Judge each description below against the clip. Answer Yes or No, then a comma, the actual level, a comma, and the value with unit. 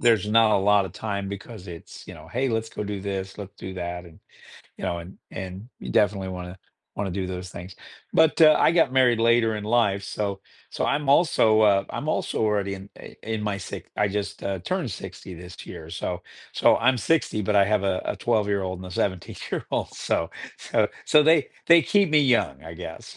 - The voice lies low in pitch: Yes, low, 100 Hz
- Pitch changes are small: No, average, 3.5 semitones